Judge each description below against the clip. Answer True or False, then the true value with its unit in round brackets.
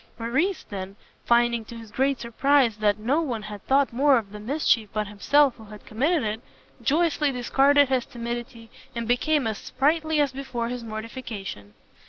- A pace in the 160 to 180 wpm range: True (170 wpm)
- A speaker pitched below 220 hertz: False (240 Hz)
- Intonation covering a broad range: False (4.3 semitones)